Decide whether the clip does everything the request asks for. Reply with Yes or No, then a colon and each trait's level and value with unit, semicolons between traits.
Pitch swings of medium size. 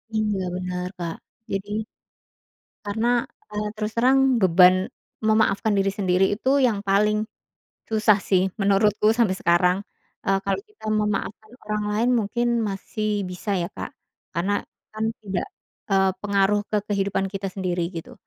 No: narrow, 1.9 semitones